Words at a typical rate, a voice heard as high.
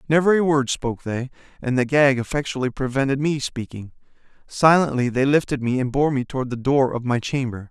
No: average, 195 wpm; low, 135 Hz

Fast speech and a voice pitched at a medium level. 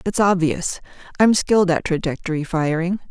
No: slow, 135 wpm; medium, 175 Hz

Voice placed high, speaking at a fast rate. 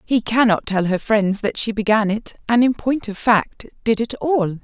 Yes: high, 220 Hz; fast, 220 wpm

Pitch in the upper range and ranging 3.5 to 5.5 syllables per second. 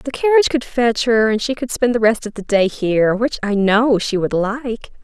Yes: high, 230 Hz; 5.1 syllables/s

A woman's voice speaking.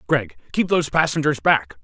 No: male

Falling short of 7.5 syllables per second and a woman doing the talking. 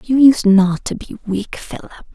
Yes: 4.6 syllables/s; female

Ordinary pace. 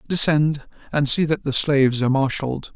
Yes: average, 175 wpm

